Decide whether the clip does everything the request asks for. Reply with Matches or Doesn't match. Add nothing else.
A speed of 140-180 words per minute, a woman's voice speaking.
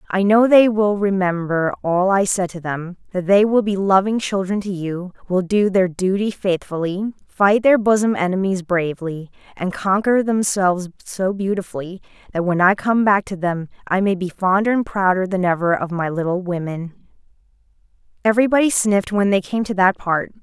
Matches